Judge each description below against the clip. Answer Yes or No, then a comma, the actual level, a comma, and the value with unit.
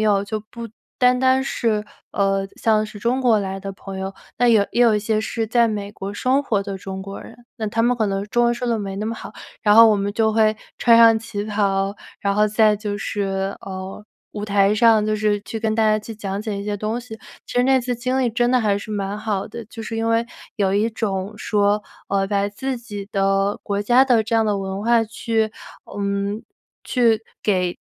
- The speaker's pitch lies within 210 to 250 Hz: Yes, high, 215 Hz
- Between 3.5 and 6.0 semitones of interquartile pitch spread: No, narrow, 2.4 semitones